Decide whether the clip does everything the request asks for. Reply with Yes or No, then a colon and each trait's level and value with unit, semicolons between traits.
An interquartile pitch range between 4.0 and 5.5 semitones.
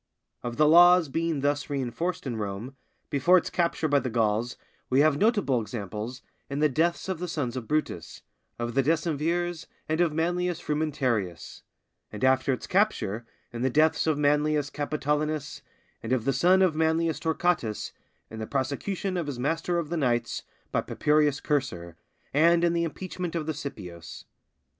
Yes: average, 4.8 semitones